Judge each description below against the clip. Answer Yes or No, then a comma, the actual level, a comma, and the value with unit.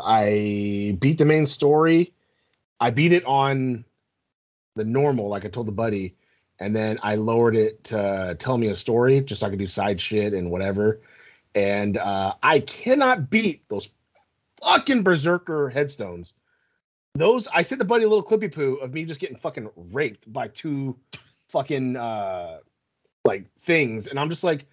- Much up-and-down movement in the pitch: Yes, wide, 7.4 semitones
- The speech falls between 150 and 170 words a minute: Yes, average, 165 wpm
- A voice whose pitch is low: Yes, low, 130 Hz